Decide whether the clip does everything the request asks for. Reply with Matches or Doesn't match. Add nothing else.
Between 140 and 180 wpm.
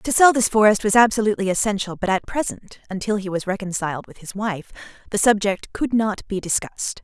Doesn't match